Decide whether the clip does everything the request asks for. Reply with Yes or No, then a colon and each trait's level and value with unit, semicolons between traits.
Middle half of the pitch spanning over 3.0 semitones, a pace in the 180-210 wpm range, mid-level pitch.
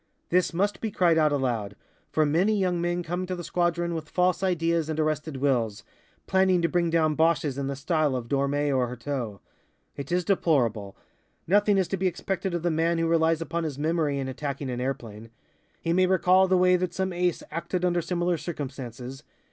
Yes: average, 4.2 semitones; average, 195 wpm; medium, 165 Hz